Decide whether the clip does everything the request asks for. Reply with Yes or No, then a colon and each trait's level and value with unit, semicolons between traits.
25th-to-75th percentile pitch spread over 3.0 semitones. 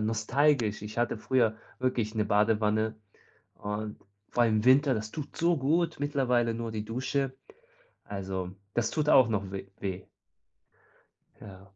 Yes: average, 3.7 semitones